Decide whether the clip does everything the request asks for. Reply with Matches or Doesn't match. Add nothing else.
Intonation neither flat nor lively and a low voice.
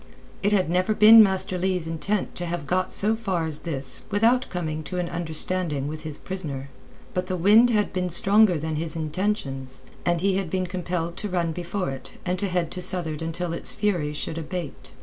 Doesn't match